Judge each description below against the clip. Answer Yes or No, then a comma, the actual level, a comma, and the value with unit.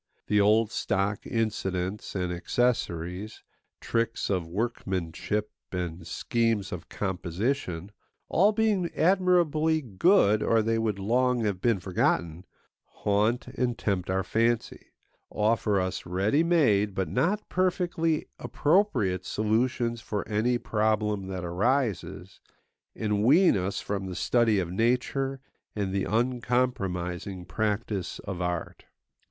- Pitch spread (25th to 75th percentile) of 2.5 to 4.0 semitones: No, average, 4.6 semitones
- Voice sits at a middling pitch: No, low, 105 Hz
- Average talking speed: No, slow, 115 wpm